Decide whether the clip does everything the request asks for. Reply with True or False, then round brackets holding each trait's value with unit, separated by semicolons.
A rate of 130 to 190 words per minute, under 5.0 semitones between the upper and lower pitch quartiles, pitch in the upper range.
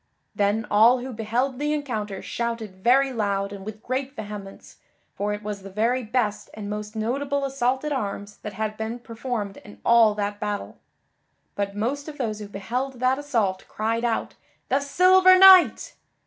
True (170 wpm; 4.0 semitones; 225 Hz)